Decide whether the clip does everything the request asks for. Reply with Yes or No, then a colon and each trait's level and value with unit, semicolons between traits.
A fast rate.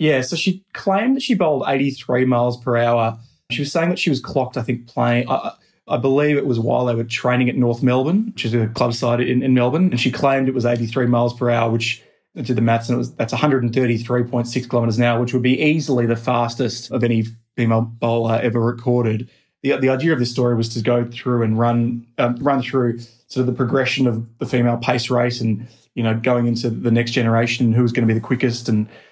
Yes: fast, 250 wpm